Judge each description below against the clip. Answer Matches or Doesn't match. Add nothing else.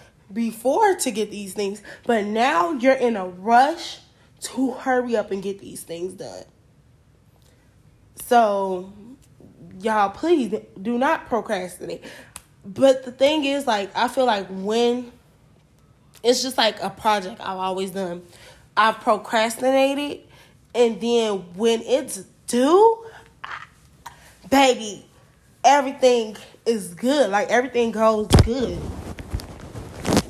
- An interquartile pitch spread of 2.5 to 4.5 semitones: Doesn't match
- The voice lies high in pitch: Matches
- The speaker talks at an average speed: Doesn't match